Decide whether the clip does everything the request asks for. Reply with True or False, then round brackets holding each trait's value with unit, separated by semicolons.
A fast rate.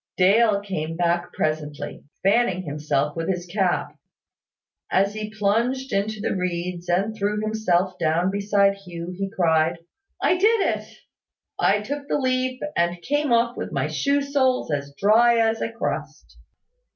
False (150 wpm)